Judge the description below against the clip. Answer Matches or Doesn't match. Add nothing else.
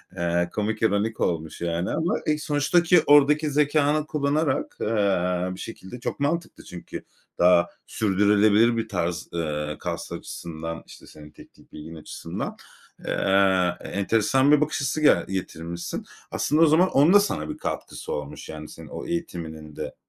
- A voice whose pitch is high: Doesn't match